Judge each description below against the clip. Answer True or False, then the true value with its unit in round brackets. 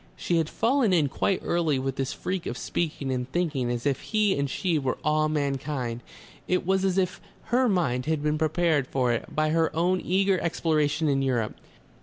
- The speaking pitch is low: False (155 Hz)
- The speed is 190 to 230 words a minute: True (195 wpm)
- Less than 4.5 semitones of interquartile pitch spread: False (4.8 semitones)